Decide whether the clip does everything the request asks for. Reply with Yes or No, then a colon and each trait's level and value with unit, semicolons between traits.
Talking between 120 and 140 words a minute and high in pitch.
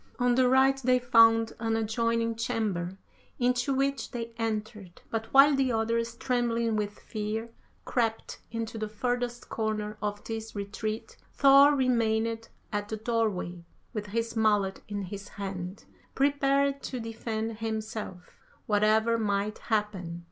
Yes: slow, 135 wpm; high, 225 Hz